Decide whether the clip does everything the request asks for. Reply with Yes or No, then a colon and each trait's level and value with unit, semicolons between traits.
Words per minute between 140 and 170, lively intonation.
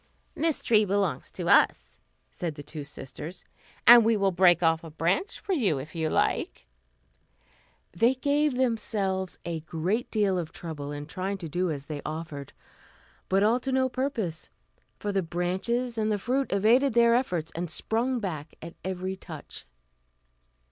Yes: average, 160 wpm; wide, 6.2 semitones